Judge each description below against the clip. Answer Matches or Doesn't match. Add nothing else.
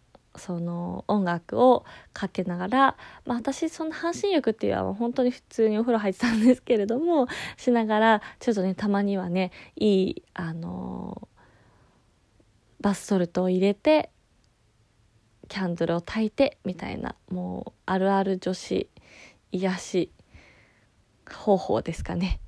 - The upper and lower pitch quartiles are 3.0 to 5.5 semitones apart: Matches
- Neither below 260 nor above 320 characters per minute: Matches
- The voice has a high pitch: Matches